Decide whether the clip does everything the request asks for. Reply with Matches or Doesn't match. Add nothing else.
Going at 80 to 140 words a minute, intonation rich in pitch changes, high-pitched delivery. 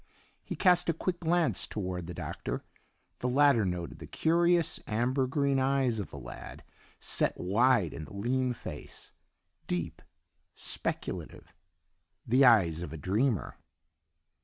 Doesn't match